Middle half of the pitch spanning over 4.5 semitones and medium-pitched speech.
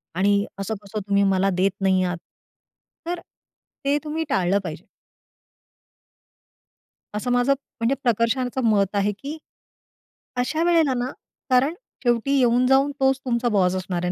No: average, 5.3 semitones; high, 235 Hz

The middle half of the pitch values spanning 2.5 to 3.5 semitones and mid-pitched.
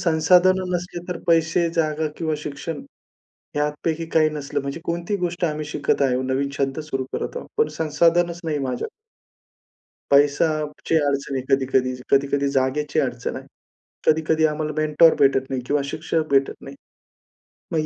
Yes: average, 2.9 semitones; medium, 155 Hz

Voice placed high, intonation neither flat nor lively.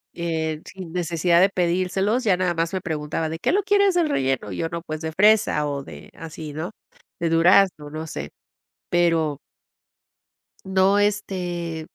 No: medium, 170 Hz; average, 3.2 semitones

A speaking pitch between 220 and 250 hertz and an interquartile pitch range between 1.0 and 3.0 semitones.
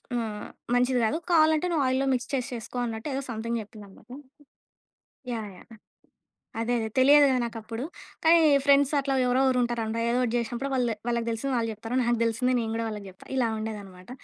Yes: high, 235 Hz; average, 2.7 semitones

